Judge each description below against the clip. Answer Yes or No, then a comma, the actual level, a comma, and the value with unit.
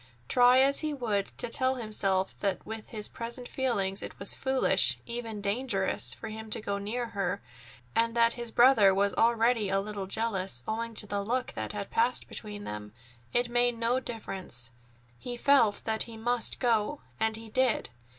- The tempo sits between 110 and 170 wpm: No, average, 180 wpm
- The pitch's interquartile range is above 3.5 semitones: No, average, 3.2 semitones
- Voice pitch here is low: No, high, 225 Hz